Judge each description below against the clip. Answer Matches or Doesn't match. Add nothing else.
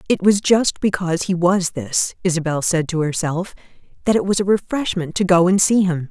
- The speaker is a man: Doesn't match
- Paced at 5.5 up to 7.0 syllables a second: Doesn't match